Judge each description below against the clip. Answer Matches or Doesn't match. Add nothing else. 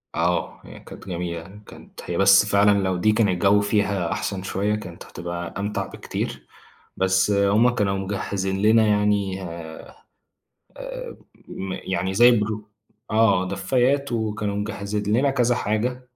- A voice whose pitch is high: Doesn't match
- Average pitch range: Doesn't match